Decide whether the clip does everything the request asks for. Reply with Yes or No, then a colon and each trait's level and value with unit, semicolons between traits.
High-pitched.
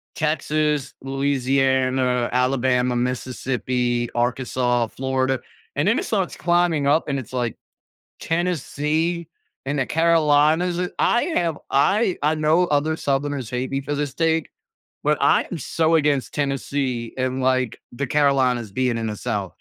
No: low, 135 Hz